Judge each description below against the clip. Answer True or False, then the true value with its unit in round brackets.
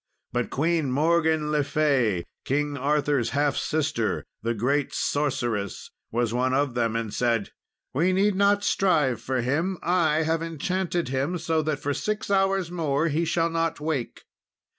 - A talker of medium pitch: True (150 Hz)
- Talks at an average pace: True (155 wpm)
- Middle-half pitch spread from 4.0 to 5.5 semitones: True (4.3 semitones)